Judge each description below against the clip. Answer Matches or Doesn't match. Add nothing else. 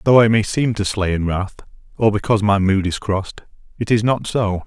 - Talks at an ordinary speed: Doesn't match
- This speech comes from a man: Matches